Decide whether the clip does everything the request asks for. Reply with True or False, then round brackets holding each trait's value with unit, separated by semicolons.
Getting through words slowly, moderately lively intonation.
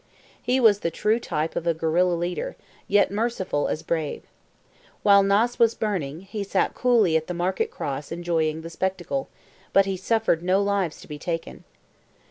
False (170 wpm; 4.0 semitones)